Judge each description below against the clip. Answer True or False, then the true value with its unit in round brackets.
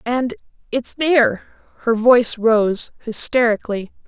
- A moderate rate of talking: False (105 wpm)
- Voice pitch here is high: True (235 Hz)